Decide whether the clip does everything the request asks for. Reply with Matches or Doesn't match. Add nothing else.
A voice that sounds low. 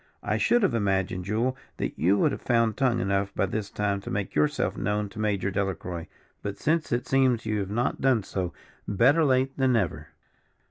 Matches